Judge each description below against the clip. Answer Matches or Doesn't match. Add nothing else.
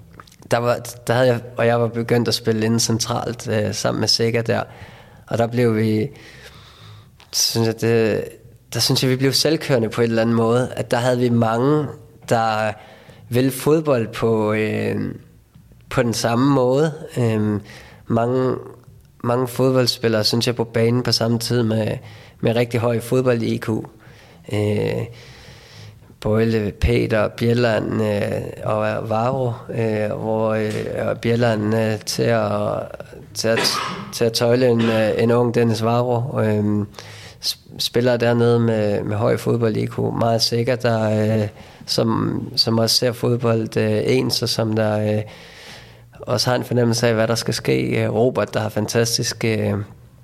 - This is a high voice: Doesn't match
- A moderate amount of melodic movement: Doesn't match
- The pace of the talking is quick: Doesn't match